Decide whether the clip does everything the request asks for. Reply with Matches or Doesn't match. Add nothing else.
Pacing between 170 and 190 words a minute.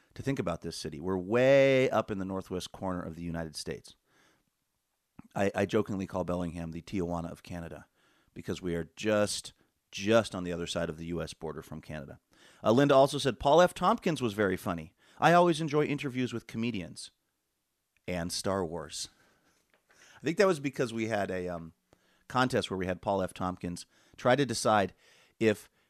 Matches